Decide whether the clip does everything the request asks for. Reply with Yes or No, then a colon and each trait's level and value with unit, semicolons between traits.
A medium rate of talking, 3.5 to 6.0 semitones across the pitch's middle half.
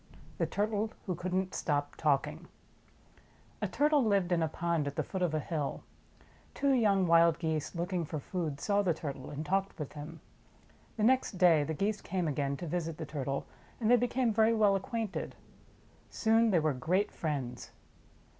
Yes: average, 185 wpm; average, 5.2 semitones